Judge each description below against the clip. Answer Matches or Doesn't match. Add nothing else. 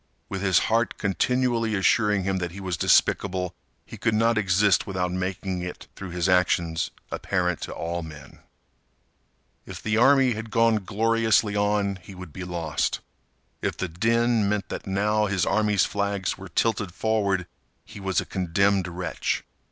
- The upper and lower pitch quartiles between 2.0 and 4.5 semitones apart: Matches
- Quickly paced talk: Doesn't match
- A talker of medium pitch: Doesn't match